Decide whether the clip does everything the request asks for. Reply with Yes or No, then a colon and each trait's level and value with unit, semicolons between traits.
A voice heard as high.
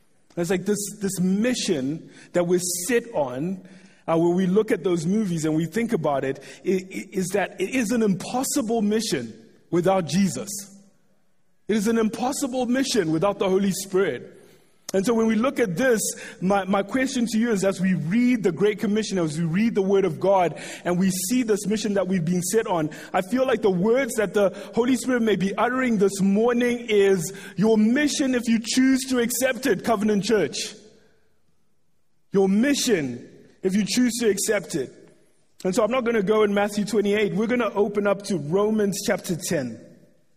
Yes: high, 205 Hz